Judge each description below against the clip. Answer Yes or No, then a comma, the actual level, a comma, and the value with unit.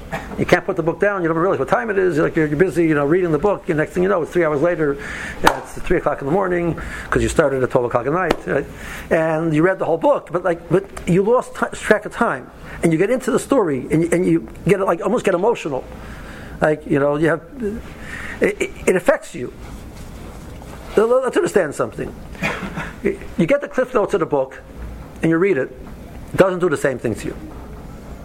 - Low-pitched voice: No, medium, 175 Hz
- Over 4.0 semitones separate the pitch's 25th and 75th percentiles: Yes, average, 4.4 semitones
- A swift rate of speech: Yes, fast, 230 wpm